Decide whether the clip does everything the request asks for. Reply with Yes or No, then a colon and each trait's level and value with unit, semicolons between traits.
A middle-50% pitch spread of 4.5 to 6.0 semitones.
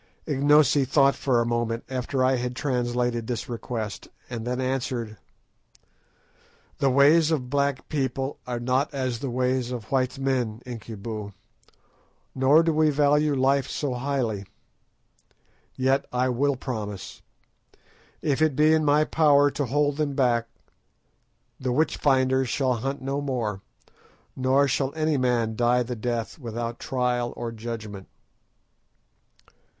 No: average, 2.9 semitones